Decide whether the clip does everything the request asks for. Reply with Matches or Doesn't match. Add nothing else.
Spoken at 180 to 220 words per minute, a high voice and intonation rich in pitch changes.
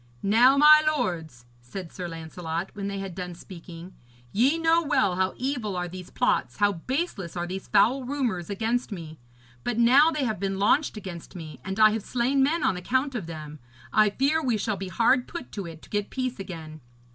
Matches